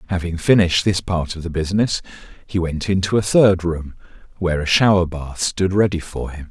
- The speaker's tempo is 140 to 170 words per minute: No, average, 195 wpm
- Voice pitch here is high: No, very low, 90 Hz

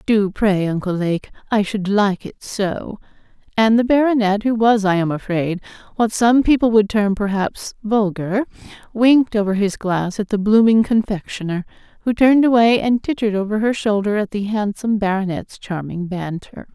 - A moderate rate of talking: Yes, average, 165 wpm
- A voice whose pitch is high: Yes, high, 210 Hz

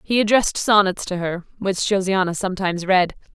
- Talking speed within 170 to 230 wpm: No, average, 160 wpm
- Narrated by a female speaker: Yes, female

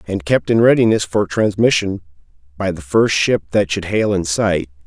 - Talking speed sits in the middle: Yes, average, 185 wpm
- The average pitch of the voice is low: Yes, very low, 95 Hz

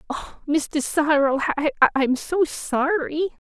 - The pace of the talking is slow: Yes, slow, 85 wpm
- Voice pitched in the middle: No, very high, 300 Hz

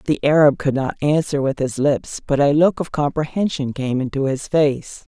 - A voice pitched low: No, medium, 145 Hz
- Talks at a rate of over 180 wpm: Yes, average, 200 wpm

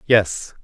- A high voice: No, low, 110 Hz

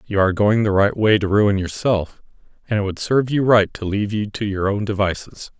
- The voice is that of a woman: No, male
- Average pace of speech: No, fast, 235 wpm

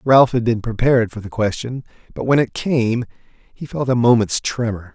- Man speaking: Yes, male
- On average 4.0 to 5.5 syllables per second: Yes, 4.9 syllables/s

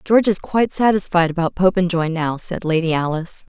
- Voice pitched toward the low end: No, medium, 180 Hz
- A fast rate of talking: No, average, 170 wpm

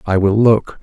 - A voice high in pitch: No, low, 105 Hz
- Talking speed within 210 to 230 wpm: Yes, fast, 215 wpm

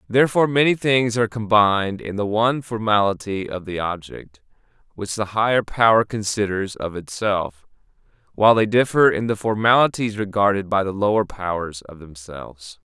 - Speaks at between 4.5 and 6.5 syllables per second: Yes, 5.2 syllables/s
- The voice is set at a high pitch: No, low, 105 Hz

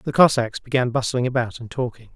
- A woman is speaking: No, male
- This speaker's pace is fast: No, average, 195 wpm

